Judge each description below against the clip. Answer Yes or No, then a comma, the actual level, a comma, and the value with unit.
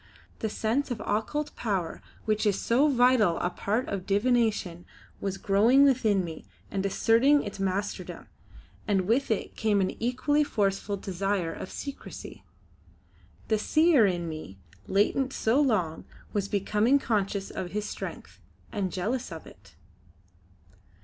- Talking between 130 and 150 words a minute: Yes, slow, 135 wpm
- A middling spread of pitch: Yes, average, 4.1 semitones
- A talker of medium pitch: No, high, 210 Hz